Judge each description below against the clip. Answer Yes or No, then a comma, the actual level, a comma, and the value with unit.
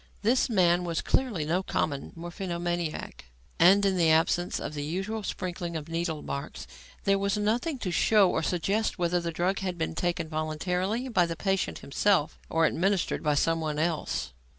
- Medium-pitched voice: Yes, medium, 175 Hz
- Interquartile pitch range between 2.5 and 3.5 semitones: Yes, average, 3.2 semitones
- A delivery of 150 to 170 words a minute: Yes, average, 165 wpm